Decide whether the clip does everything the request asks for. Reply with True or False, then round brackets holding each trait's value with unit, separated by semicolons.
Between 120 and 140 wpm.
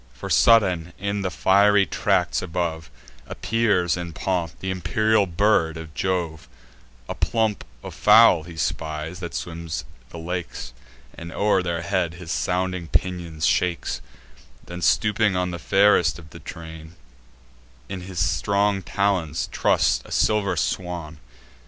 True (135 wpm)